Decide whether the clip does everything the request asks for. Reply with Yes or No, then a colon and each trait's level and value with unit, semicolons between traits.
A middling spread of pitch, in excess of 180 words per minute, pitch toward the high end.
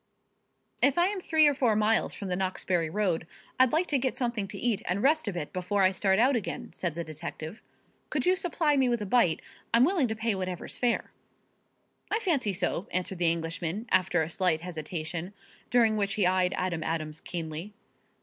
No: wide, 5.8 semitones; average, 200 wpm; high, 195 Hz